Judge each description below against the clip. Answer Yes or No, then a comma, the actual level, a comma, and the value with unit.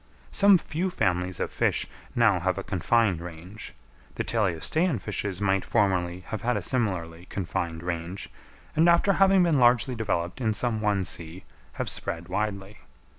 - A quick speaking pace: No, average, 155 wpm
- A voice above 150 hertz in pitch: No, low, 100 Hz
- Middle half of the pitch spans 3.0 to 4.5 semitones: No, average, 5.2 semitones